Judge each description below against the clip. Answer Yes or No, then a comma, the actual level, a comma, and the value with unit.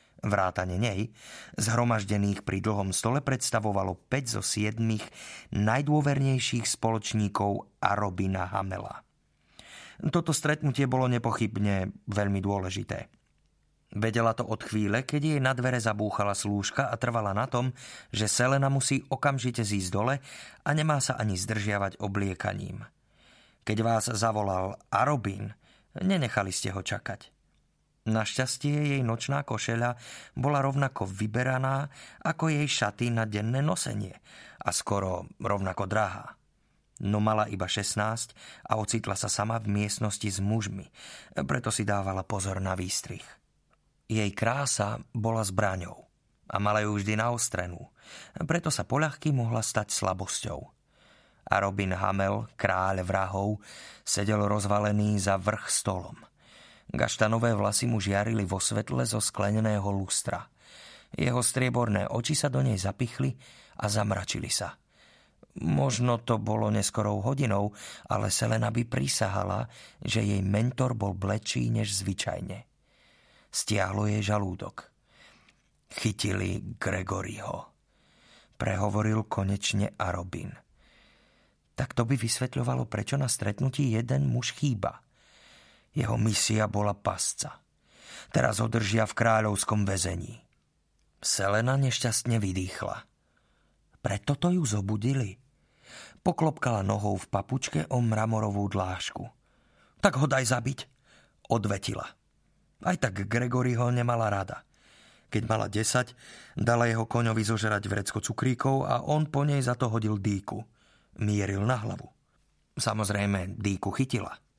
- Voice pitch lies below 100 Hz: No, low, 110 Hz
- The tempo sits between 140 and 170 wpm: No, average, 120 wpm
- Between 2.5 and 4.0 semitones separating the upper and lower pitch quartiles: Yes, average, 3.6 semitones